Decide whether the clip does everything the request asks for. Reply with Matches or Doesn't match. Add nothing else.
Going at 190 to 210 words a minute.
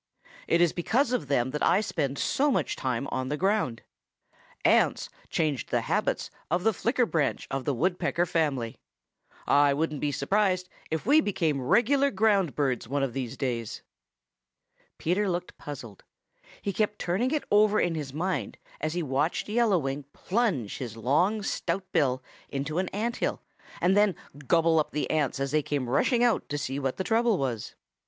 Doesn't match